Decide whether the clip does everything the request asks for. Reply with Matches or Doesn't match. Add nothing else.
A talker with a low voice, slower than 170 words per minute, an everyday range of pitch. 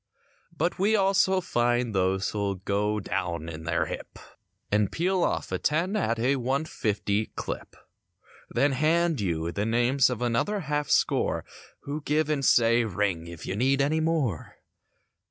Doesn't match